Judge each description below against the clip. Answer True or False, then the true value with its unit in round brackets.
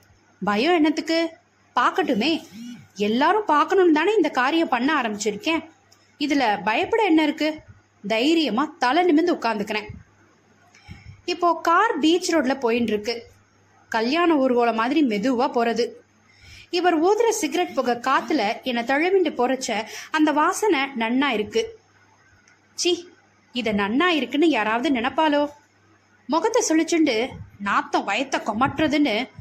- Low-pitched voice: False (295 Hz)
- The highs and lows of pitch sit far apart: True (6.0 semitones)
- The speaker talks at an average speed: True (105 wpm)